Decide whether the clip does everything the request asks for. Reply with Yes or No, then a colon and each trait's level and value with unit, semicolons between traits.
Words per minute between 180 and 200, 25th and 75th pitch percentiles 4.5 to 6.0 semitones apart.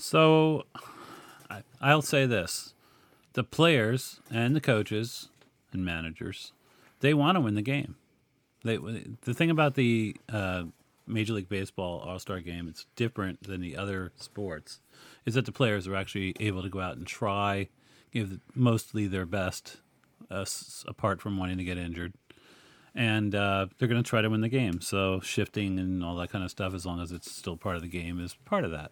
Yes: average, 195 wpm; average, 4.9 semitones